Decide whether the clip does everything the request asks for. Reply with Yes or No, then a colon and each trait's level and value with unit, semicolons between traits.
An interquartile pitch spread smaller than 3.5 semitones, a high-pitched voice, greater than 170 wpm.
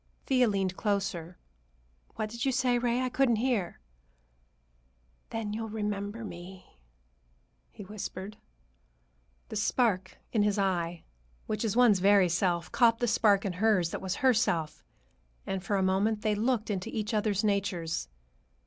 No: average, 3.1 semitones; high, 205 Hz; average, 145 wpm